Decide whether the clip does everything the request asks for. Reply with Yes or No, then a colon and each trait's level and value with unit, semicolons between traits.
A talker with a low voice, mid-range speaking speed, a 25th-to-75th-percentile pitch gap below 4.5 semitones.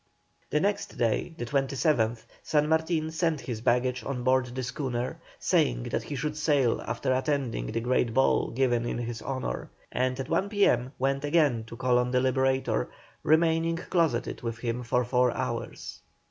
Yes: low, 130 Hz; average, 170 wpm; average, 3.8 semitones